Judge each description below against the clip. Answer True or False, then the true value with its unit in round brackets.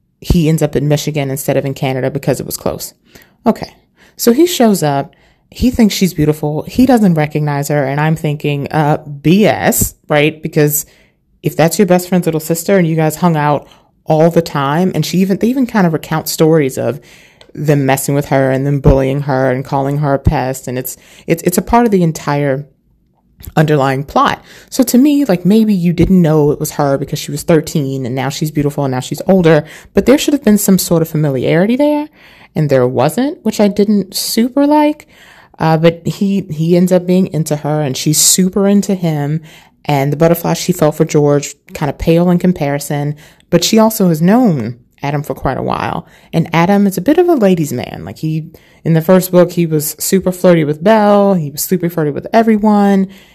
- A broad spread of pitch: False (4.6 semitones)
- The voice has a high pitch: False (160 Hz)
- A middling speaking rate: False (210 wpm)